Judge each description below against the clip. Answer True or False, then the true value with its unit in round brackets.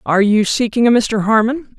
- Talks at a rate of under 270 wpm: True (200 wpm)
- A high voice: True (225 Hz)